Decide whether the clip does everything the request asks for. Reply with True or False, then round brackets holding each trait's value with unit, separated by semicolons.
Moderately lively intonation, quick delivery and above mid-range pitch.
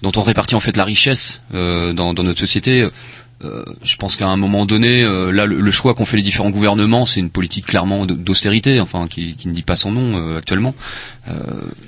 False (3.7 semitones; 225 wpm; 100 Hz)